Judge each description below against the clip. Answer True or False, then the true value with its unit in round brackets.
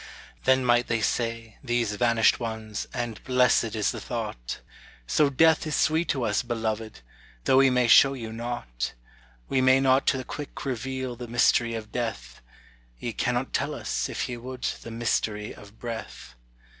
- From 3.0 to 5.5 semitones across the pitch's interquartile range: False (2.6 semitones)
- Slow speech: False (170 wpm)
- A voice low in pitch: True (120 Hz)